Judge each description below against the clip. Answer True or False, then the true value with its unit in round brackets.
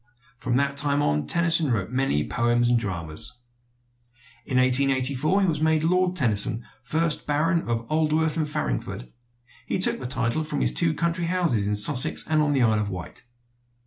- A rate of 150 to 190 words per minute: True (175 wpm)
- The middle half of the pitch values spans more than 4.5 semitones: True (5.6 semitones)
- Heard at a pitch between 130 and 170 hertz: True (135 Hz)